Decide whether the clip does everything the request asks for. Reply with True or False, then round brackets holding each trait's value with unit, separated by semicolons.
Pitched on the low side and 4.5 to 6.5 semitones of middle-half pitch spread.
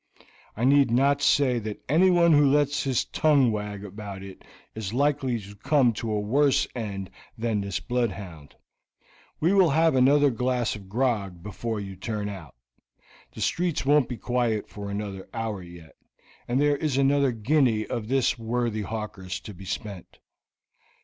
True (115 Hz; 5.1 semitones)